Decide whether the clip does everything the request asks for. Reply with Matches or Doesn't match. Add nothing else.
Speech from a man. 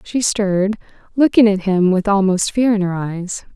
Doesn't match